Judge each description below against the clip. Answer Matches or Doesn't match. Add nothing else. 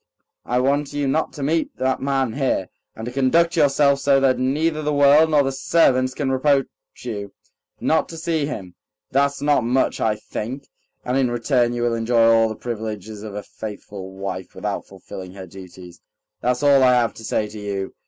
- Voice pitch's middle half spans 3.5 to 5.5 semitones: Matches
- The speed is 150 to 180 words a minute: Doesn't match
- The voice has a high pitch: Doesn't match